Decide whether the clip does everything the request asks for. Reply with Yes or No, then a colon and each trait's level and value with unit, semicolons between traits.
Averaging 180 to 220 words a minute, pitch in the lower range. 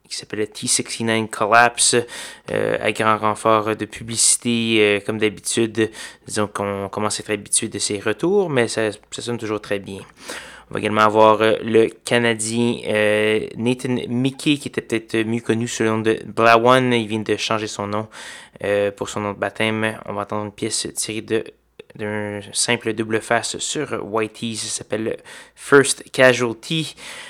No: average, 170 wpm; low, 110 Hz